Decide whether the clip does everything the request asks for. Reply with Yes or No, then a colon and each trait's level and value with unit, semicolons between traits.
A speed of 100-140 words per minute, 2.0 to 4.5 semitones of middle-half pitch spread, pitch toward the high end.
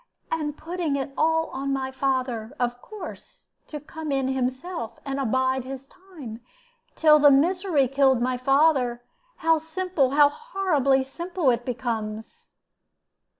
Yes: slow, 135 wpm; average, 3.9 semitones; very high, 275 Hz